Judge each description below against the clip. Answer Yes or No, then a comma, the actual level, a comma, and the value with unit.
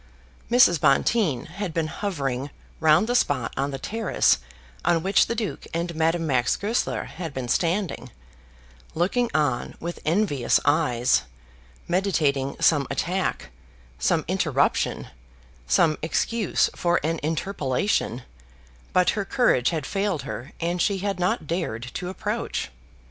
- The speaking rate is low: Yes, slow, 130 wpm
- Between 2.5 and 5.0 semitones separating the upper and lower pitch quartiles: No, wide, 5.5 semitones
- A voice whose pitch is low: No, medium, 165 Hz